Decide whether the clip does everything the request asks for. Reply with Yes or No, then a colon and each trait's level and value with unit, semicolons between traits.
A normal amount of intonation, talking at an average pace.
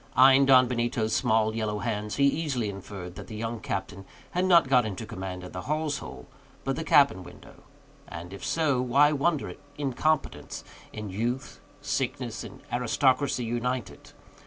Yes: average, 4.6 semitones; average, 160 wpm